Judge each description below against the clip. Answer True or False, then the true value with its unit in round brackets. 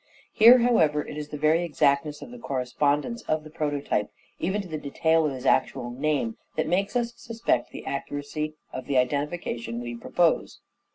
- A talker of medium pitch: True (150 Hz)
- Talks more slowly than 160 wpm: False (175 wpm)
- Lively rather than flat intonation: False (3.5 semitones)